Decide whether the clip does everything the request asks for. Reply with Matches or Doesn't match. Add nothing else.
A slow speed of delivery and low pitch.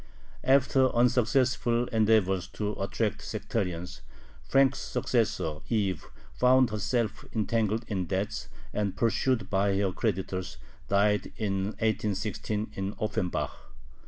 Matches